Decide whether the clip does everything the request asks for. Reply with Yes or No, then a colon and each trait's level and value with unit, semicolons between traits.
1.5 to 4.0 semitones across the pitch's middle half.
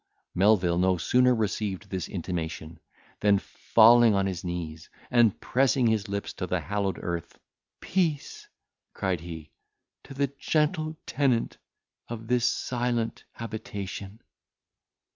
No: average, 4.8 semitones